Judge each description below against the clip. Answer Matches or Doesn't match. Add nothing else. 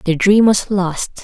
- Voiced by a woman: Matches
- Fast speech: Doesn't match